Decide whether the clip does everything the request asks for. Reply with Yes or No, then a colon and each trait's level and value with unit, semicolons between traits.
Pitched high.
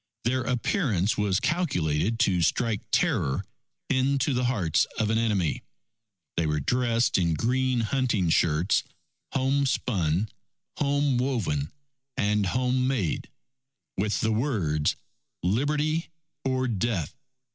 No: low, 115 Hz